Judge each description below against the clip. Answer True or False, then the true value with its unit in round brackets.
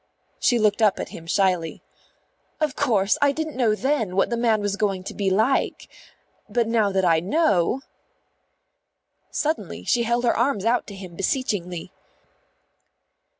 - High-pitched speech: True (215 Hz)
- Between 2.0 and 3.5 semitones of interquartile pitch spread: False (4.2 semitones)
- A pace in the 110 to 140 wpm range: False (155 wpm)